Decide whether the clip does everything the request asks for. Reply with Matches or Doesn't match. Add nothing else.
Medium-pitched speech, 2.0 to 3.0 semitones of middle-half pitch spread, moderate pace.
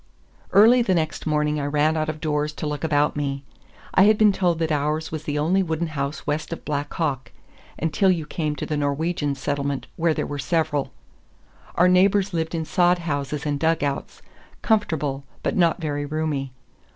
Matches